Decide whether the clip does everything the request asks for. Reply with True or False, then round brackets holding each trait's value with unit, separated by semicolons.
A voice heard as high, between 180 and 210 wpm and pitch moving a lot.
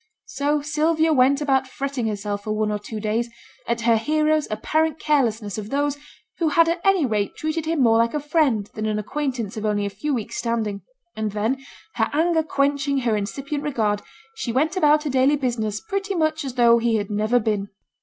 True (255 Hz; 200 wpm; 5.7 semitones)